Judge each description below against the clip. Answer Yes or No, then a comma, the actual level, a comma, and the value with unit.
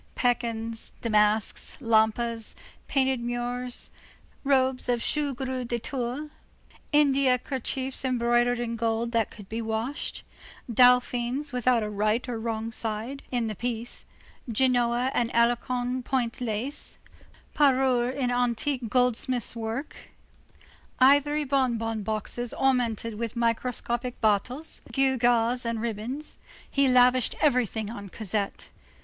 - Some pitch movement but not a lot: No, narrow, 2.2 semitones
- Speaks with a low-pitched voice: No, high, 240 Hz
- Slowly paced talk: Yes, slow, 115 wpm